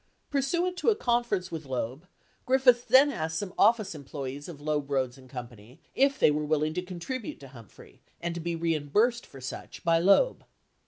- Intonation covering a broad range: Yes, wide, 8.7 semitones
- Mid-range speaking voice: Yes, medium, 165 Hz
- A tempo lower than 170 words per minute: No, average, 190 wpm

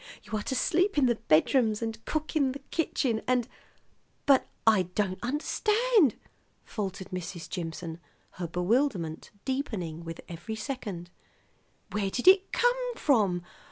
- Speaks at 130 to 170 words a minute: Yes, average, 140 wpm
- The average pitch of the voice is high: Yes, high, 225 Hz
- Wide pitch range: Yes, wide, 7.7 semitones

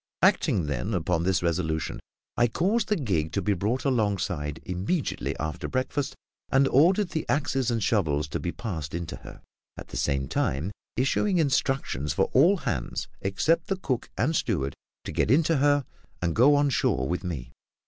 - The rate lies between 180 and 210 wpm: No, average, 170 wpm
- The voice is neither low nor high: No, low, 105 Hz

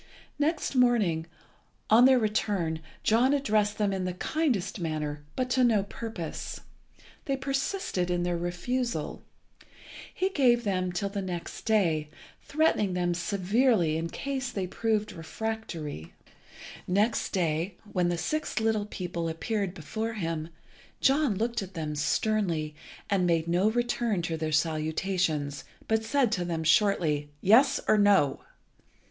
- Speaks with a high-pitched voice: Yes, high, 195 Hz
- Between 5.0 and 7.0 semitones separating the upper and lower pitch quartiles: Yes, average, 5.3 semitones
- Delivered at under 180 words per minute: Yes, average, 140 wpm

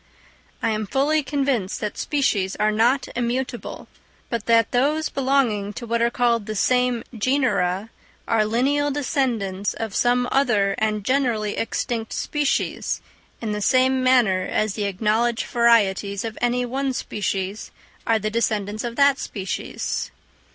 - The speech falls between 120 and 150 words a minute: Yes, average, 140 wpm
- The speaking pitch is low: No, high, 230 Hz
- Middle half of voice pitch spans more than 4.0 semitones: No, average, 3.5 semitones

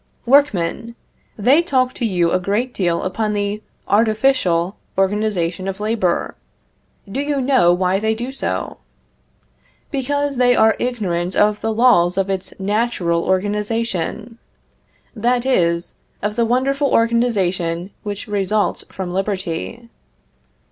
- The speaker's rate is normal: No, slow, 120 wpm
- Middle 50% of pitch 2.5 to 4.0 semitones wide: No, average, 4.5 semitones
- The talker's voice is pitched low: No, high, 210 Hz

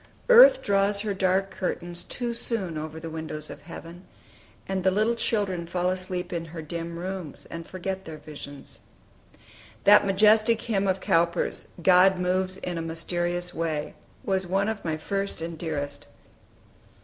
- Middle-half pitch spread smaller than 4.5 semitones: Yes, average, 2.9 semitones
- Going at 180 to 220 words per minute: No, average, 155 wpm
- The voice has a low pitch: No, medium, 180 Hz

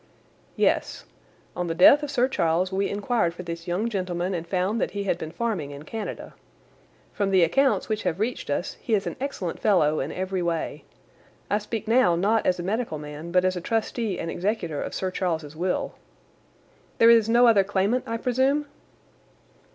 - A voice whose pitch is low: No, high, 190 Hz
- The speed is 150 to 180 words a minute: No, average, 190 wpm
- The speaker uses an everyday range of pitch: Yes, average, 4.7 semitones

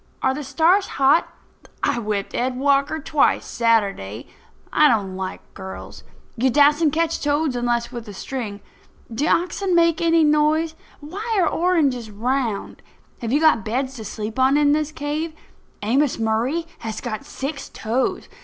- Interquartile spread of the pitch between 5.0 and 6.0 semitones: Yes, average, 5.3 semitones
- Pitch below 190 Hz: No, very high, 270 Hz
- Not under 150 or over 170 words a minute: Yes, average, 155 wpm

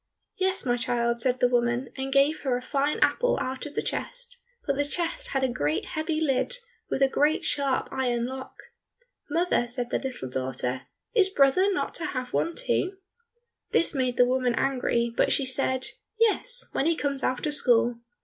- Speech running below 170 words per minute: No, average, 190 wpm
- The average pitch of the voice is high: Yes, very high, 265 Hz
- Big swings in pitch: No, average, 4.2 semitones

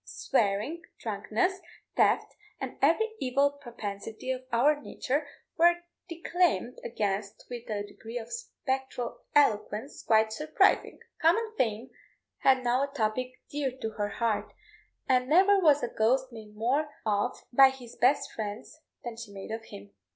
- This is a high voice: Yes, very high, 250 Hz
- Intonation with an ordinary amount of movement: Yes, average, 4.8 semitones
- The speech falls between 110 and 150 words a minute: Yes, average, 145 wpm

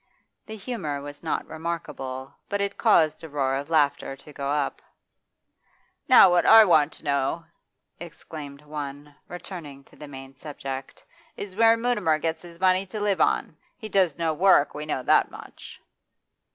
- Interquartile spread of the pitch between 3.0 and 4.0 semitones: No, average, 4.6 semitones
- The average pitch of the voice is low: No, medium, 155 Hz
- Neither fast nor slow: Yes, average, 165 wpm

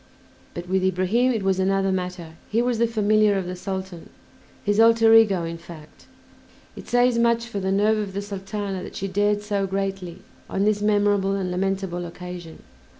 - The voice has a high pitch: Yes, high, 195 Hz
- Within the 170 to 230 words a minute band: Yes, average, 180 wpm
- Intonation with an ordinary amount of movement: No, narrow, 2.2 semitones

